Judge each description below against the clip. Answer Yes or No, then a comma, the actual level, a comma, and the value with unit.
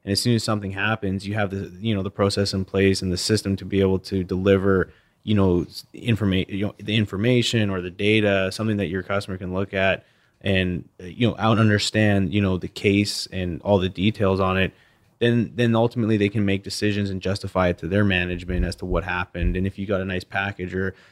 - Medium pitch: No, low, 100 Hz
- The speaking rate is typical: No, fast, 225 wpm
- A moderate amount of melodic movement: No, narrow, 1.9 semitones